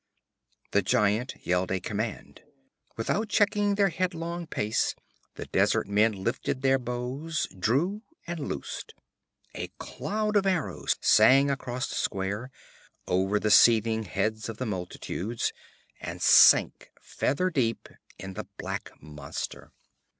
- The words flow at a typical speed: No, slow, 130 wpm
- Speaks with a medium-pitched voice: No, low, 120 Hz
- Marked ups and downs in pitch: Yes, wide, 8.0 semitones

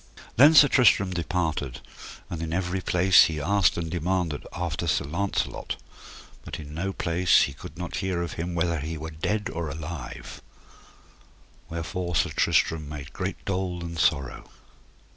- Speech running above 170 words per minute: No, average, 155 wpm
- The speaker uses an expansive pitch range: No, average, 2.7 semitones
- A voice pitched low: Yes, very low, 85 Hz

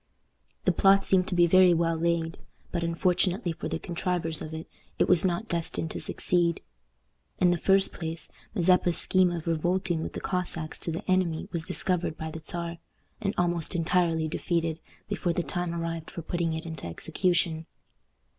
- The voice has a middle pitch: Yes, medium, 170 Hz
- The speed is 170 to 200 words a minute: Yes, average, 175 wpm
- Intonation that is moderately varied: No, narrow, 1.8 semitones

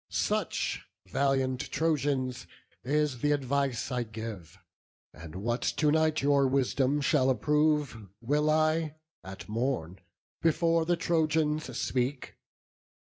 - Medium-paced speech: No, slow, 110 wpm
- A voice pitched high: No, medium, 140 Hz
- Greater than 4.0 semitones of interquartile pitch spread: No, average, 3.7 semitones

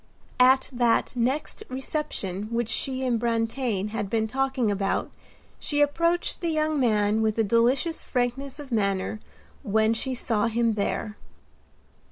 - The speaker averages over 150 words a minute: No, average, 140 wpm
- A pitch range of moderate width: Yes, average, 3.5 semitones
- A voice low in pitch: No, high, 235 Hz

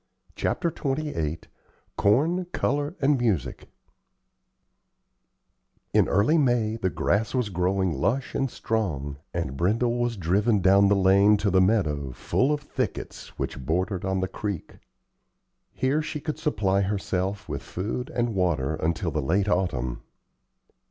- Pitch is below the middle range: Yes, low, 100 Hz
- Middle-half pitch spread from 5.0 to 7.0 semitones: Yes, wide, 5.4 semitones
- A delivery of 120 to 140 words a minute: Yes, slow, 135 wpm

